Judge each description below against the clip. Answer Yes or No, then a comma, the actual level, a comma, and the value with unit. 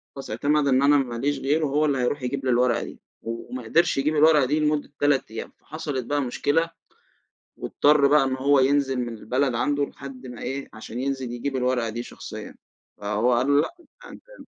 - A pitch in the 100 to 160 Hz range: Yes, low, 135 Hz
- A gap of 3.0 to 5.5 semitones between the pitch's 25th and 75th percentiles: No, narrow, 2.6 semitones